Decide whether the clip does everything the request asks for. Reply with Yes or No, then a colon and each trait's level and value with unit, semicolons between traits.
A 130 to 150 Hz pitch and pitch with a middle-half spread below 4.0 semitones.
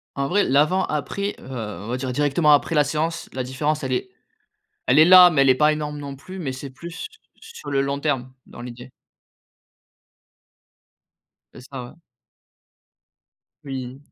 Yes: medium, 140 Hz; average, 2.9 semitones